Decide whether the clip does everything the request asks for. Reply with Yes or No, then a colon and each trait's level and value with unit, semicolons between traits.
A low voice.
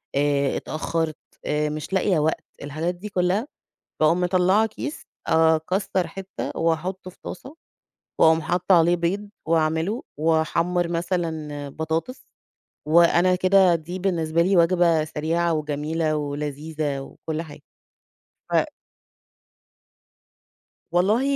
No: medium, 165 Hz